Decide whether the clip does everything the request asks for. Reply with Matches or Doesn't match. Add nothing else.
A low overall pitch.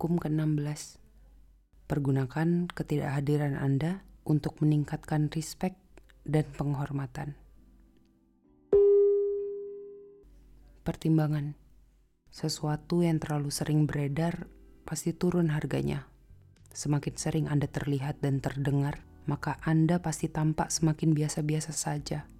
Doesn't match